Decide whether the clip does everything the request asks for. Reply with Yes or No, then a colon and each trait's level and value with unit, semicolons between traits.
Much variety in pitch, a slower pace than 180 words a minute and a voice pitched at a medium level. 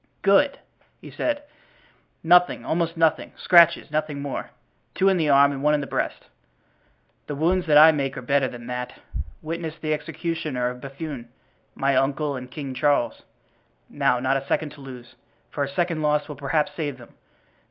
No: average, 3.0 semitones; average, 165 wpm; medium, 145 Hz